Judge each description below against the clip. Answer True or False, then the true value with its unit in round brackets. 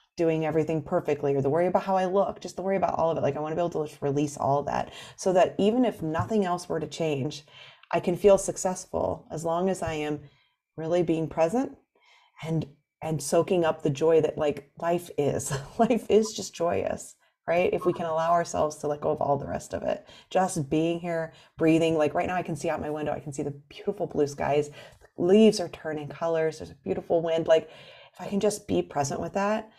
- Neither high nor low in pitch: True (165 Hz)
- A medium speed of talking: False (235 wpm)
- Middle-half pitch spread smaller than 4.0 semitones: True (3.3 semitones)